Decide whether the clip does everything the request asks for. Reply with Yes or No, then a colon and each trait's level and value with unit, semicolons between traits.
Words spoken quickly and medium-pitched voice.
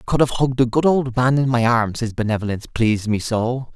No: fast, 255 wpm; low, 120 Hz